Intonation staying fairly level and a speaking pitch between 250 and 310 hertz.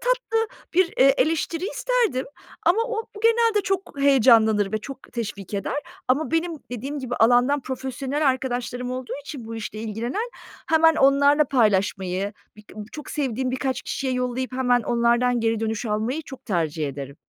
No: average, 4.9 semitones; very high, 255 Hz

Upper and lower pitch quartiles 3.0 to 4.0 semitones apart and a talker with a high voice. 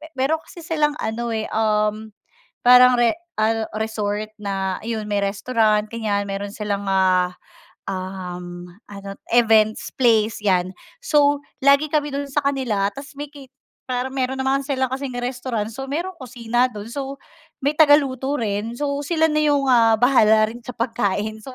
No: average, 4.4 semitones; high, 235 Hz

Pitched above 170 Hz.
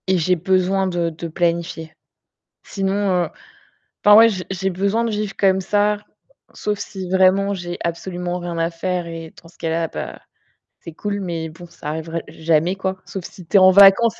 Yes: medium, 185 Hz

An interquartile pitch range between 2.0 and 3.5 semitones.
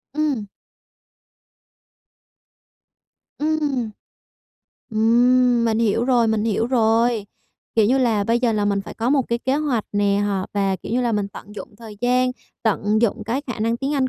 Yes: average, 3.1 semitones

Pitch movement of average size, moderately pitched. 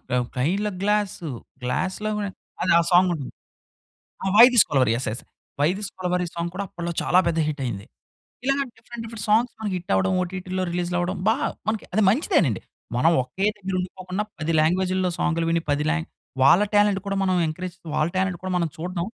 Yes: average, 3.2 semitones; medium, 180 Hz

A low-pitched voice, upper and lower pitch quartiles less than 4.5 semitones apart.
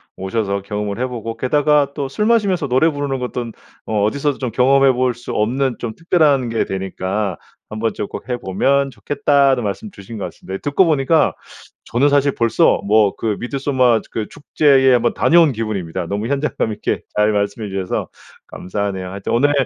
No: low, 120 Hz; average, 5.1 semitones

